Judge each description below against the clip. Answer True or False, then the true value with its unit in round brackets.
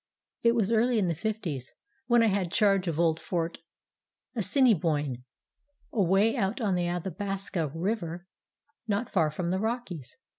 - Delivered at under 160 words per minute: True (145 wpm)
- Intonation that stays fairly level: False (4.5 semitones)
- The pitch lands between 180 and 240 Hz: True (190 Hz)